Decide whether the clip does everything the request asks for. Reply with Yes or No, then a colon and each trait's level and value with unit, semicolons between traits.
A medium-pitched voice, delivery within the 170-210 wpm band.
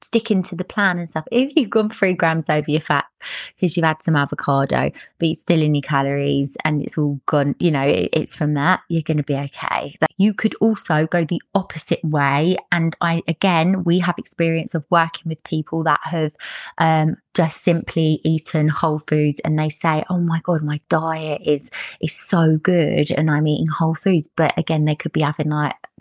Yes: medium, 160 Hz; fast, 205 wpm